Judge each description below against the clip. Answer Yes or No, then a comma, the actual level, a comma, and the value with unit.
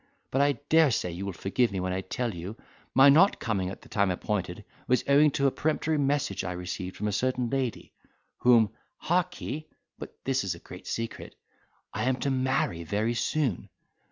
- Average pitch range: No, wide, 6.3 semitones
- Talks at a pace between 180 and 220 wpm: Yes, average, 190 wpm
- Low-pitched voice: Yes, low, 120 Hz